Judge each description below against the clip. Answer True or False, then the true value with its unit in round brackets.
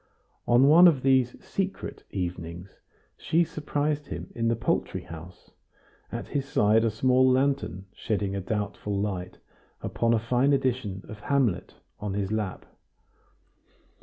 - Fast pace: False (135 wpm)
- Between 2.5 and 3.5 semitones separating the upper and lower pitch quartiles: False (5.4 semitones)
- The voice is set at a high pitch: False (115 Hz)